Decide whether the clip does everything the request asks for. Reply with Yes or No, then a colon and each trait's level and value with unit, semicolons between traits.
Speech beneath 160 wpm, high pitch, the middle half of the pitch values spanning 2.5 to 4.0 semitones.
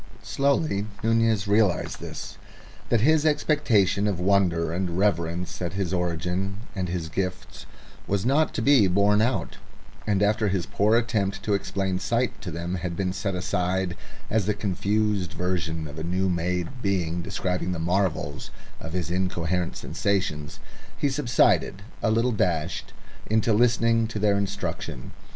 No: average, 150 wpm; very low, 95 Hz; average, 3.3 semitones